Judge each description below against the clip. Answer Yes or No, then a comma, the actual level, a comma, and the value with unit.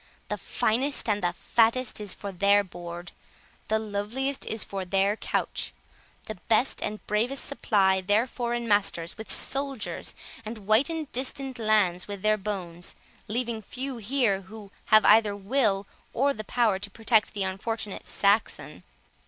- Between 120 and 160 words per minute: Yes, average, 145 wpm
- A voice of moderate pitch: No, high, 215 Hz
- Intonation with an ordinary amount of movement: Yes, average, 3.1 semitones